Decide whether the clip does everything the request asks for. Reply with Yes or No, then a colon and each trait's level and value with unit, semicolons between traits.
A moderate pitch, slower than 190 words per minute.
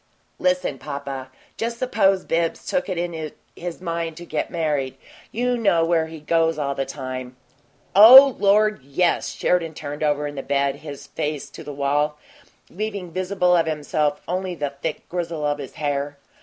Yes: medium, 160 Hz; average, 170 wpm